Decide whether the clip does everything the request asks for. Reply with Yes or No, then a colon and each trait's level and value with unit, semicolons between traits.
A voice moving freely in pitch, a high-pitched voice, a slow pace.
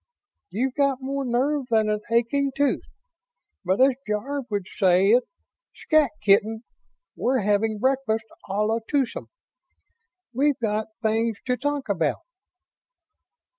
No: average, 4.3 semitones; high, 235 Hz; slow, 125 wpm